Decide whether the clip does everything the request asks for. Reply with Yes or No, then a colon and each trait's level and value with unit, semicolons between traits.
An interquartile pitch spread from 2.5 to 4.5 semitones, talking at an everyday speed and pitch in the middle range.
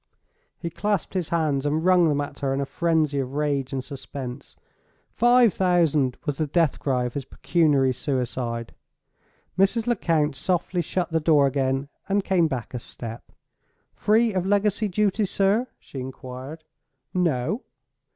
No: wide, 5.5 semitones; average, 150 wpm; medium, 155 Hz